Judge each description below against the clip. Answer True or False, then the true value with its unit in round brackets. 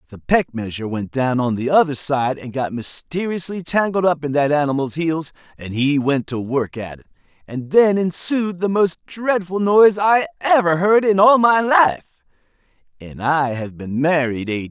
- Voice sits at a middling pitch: True (155 Hz)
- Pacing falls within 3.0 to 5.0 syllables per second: True (4.9 syllables/s)